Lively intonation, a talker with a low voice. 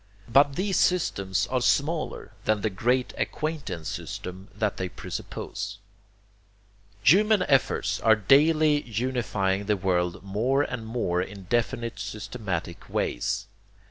Yes: wide, 5.7 semitones; low, 110 Hz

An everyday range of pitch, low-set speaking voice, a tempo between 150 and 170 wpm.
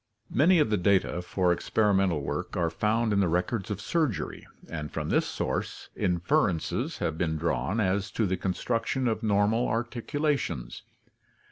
Yes: average, 4.6 semitones; low, 100 Hz; average, 160 wpm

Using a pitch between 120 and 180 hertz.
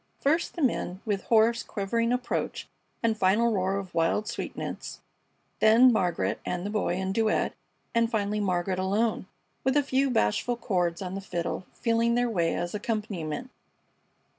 No: high, 210 Hz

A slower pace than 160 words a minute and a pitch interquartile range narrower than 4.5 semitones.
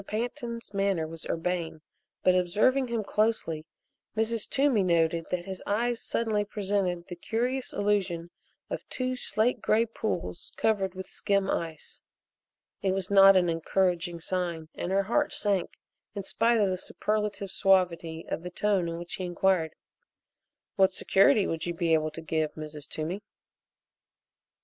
Yes: average, 150 wpm; average, 3.9 semitones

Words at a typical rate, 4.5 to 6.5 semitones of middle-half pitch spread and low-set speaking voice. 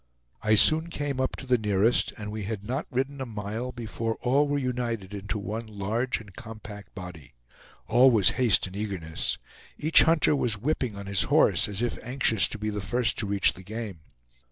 No: average, 195 wpm; average, 3.8 semitones; low, 110 Hz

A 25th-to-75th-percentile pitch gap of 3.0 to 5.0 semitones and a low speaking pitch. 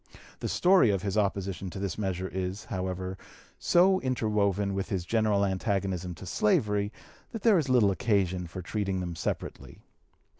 No: narrow, 2.4 semitones; low, 100 Hz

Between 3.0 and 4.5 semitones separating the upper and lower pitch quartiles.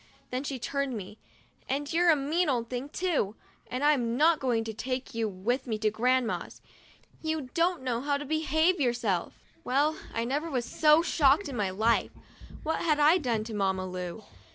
No: average, 4.9 semitones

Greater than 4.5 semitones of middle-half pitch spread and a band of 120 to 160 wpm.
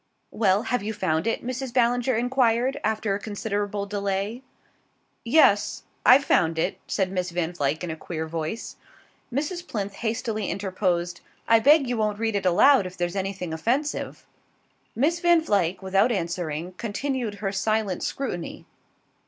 Yes: average, 4.9 semitones; average, 150 wpm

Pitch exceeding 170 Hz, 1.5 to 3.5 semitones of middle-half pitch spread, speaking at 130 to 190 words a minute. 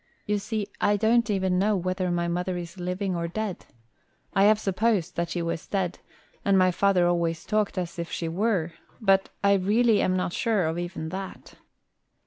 Yes: medium, 185 Hz; average, 2.9 semitones; average, 185 wpm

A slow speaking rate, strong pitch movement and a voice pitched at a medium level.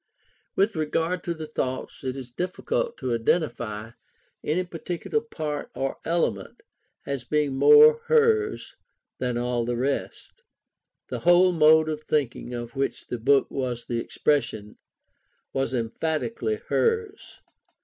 Yes: slow, 130 wpm; wide, 6.4 semitones; medium, 150 Hz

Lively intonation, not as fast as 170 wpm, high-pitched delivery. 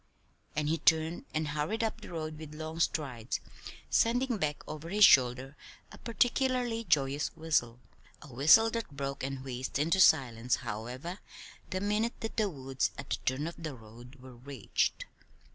No: wide, 6.2 semitones; average, 160 wpm; medium, 150 Hz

